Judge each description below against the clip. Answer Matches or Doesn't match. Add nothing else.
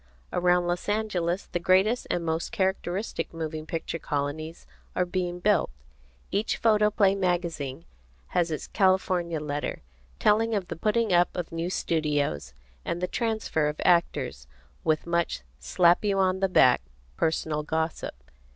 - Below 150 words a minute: Matches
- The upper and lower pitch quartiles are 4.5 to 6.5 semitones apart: Doesn't match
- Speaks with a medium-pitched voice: Matches